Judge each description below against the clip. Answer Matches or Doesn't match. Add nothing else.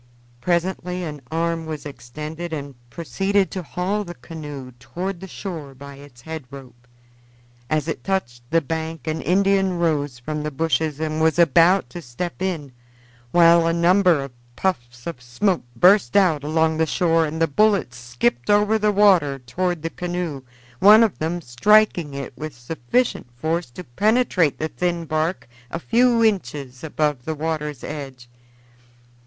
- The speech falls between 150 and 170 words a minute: Matches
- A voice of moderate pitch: Matches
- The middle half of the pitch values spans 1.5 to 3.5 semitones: Doesn't match